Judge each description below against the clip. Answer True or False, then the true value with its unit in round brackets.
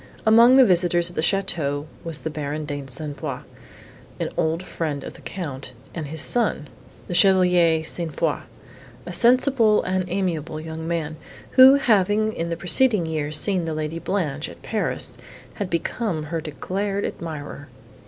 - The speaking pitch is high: False (170 Hz)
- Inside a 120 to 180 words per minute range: True (160 wpm)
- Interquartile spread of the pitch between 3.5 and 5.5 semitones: True (4.2 semitones)